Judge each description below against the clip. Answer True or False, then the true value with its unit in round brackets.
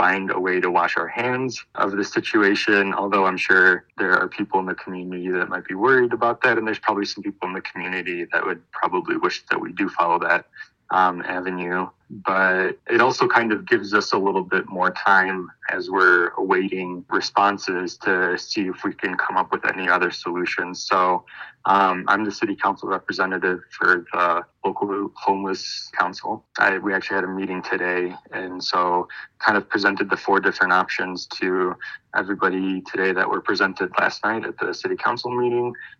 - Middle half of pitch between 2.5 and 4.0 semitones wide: False (5.1 semitones)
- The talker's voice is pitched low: True (95 Hz)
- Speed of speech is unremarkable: True (185 wpm)